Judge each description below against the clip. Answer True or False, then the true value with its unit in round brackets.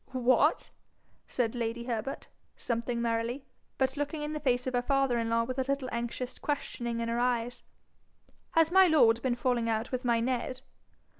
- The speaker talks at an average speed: True (175 wpm)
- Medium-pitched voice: False (245 Hz)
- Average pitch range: False (2.1 semitones)